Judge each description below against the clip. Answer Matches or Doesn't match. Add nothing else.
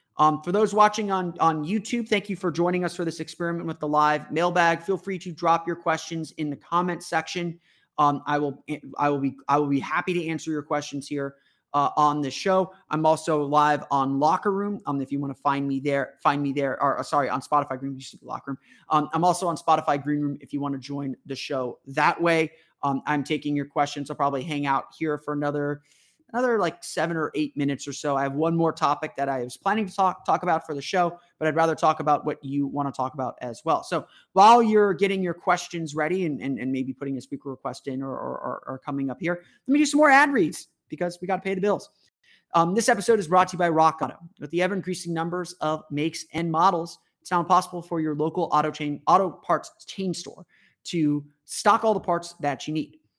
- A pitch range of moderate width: Matches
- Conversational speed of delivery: Doesn't match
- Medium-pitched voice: Matches